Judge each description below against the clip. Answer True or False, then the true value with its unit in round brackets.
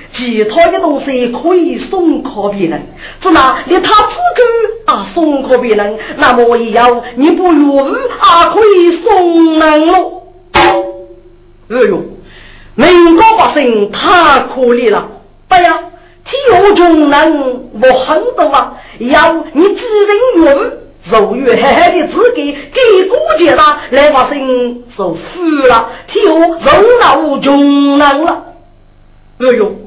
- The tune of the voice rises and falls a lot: True (6.0 semitones)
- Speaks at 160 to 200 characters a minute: True (180 characters per minute)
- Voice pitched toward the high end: True (320 Hz)